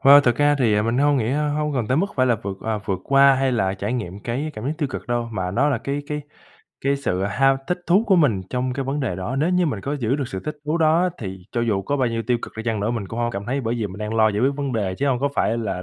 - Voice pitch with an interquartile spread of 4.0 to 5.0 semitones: Yes, average, 4.7 semitones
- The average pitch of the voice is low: Yes, low, 125 Hz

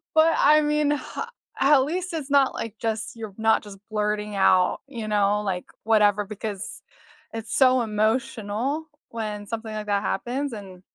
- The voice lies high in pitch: Yes, high, 220 Hz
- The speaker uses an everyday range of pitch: Yes, average, 4.4 semitones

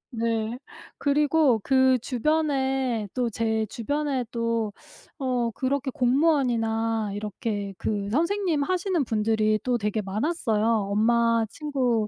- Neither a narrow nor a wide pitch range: Yes, average, 4.2 semitones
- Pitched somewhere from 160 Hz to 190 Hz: No, high, 235 Hz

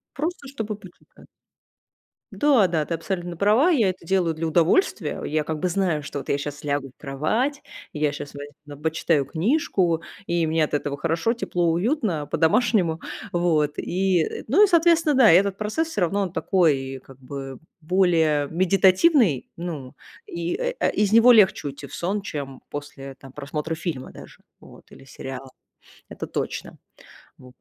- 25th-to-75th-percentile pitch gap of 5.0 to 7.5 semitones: Yes, wide, 5.6 semitones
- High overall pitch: No, medium, 170 Hz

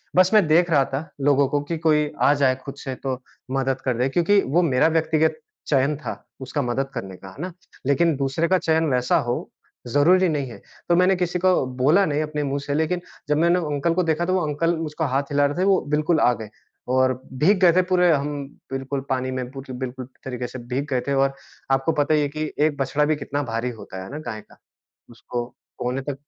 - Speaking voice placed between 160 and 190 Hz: No, medium, 145 Hz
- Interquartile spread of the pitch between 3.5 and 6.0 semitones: Yes, average, 3.8 semitones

